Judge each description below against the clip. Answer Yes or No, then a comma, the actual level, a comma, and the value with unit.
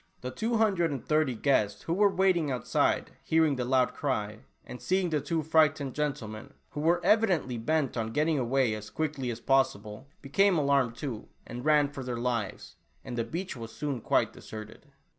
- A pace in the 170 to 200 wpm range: Yes, average, 185 wpm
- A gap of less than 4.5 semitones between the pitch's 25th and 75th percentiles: No, average, 4.8 semitones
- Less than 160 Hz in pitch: Yes, medium, 140 Hz